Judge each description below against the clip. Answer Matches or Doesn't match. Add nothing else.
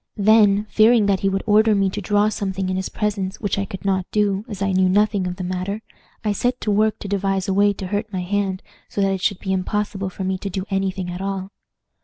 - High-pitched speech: Matches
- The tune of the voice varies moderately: Doesn't match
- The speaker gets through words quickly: Matches